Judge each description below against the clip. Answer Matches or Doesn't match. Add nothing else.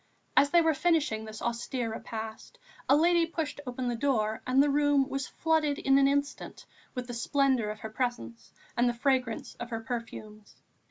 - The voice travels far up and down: Doesn't match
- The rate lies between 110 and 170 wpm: Doesn't match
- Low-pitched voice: Doesn't match